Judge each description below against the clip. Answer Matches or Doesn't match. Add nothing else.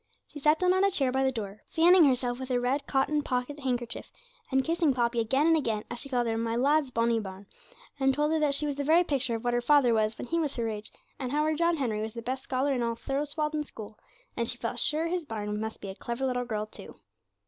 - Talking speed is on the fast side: Matches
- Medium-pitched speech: Doesn't match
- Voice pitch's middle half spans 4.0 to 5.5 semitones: Matches